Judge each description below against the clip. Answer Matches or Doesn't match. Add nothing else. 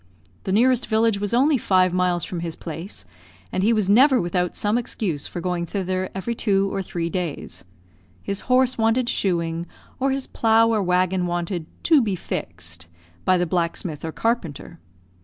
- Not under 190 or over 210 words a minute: Doesn't match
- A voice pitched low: Doesn't match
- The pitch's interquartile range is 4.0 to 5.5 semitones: Matches